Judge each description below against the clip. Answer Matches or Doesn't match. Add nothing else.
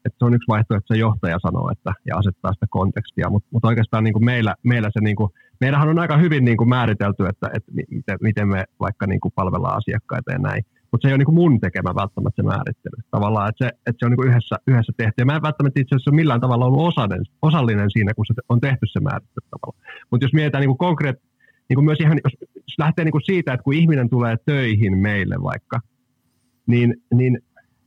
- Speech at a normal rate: Doesn't match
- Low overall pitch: Matches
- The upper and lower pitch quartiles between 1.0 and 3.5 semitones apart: Doesn't match